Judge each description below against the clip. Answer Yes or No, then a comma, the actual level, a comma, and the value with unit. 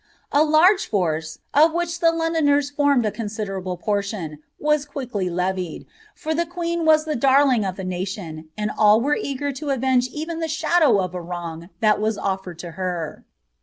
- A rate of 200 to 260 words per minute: No, average, 175 wpm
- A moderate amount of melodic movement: No, wide, 8.5 semitones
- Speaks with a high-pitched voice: Yes, high, 235 Hz